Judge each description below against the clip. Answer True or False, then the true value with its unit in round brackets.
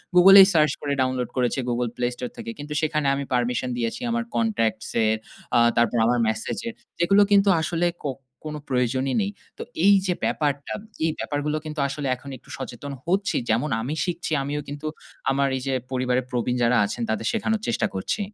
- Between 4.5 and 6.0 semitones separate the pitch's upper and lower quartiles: True (5.1 semitones)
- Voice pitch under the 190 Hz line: True (140 Hz)